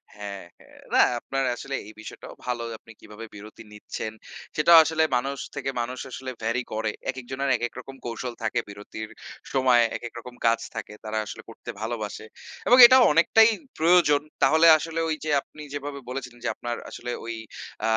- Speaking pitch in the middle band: No, low, 125 Hz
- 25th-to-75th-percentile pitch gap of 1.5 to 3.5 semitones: No, average, 4.1 semitones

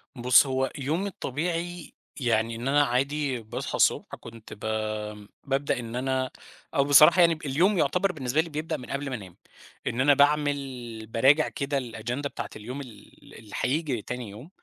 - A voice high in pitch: No, low, 135 Hz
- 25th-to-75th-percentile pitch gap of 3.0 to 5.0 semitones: Yes, average, 3.6 semitones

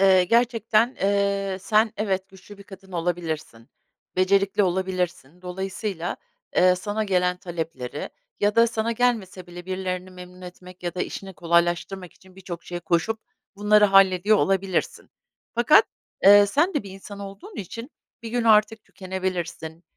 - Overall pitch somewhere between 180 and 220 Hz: Yes, high, 190 Hz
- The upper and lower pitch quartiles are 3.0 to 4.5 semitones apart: No, narrow, 2.5 semitones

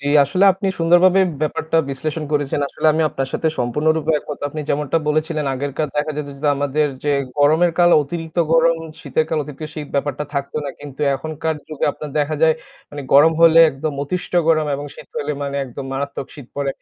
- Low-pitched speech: No, medium, 150 Hz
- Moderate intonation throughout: No, narrow, 2.2 semitones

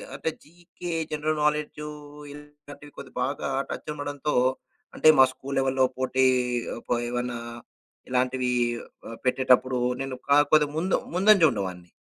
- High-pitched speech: No, medium, 140 Hz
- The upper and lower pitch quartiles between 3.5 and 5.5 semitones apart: No, average, 2.8 semitones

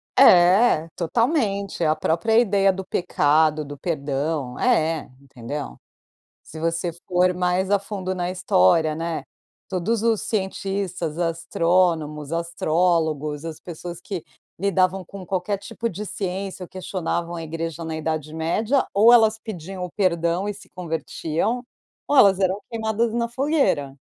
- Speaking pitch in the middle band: Yes, medium, 180 Hz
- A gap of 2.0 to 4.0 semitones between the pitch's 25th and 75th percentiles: Yes, average, 3.6 semitones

